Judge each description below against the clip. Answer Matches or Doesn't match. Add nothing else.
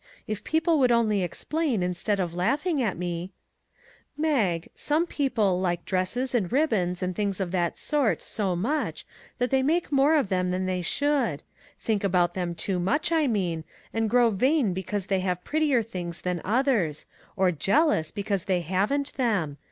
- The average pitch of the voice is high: Matches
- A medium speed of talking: Matches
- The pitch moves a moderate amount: Doesn't match